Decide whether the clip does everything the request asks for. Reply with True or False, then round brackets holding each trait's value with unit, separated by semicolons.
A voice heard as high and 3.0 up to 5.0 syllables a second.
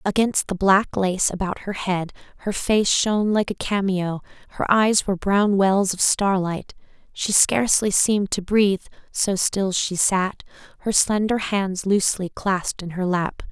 True (195 Hz; 4.4 syllables/s)